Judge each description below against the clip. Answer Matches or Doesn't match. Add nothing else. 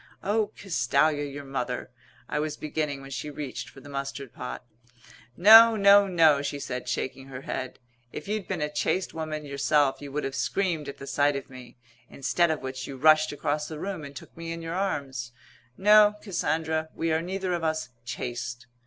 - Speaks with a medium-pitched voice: Matches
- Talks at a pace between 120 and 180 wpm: Doesn't match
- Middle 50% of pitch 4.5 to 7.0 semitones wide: Doesn't match